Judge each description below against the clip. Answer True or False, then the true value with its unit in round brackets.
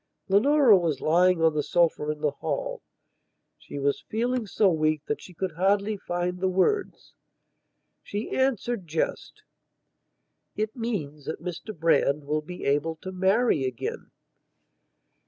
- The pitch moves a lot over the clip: True (5.7 semitones)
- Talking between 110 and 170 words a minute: True (135 wpm)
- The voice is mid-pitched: True (180 Hz)